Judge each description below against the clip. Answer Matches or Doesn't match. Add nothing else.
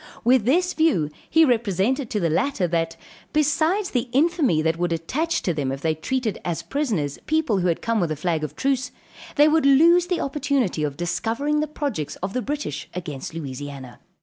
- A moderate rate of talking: Matches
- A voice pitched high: Matches